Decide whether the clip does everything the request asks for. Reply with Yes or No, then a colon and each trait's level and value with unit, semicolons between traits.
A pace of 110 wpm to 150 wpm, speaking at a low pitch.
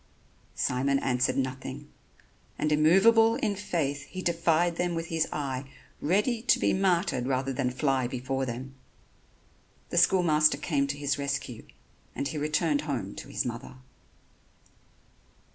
No: average, 140 wpm; medium, 145 Hz